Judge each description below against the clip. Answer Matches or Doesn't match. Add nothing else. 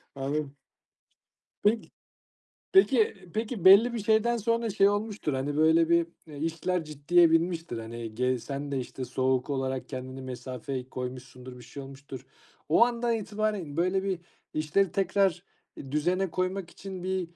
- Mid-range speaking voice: Matches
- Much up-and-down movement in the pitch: Matches